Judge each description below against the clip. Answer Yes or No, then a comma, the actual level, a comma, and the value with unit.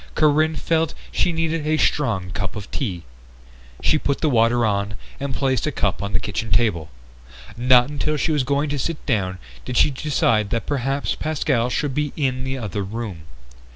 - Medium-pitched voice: No, low, 130 Hz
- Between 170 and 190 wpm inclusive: Yes, average, 185 wpm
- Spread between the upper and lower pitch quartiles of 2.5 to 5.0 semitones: No, wide, 5.5 semitones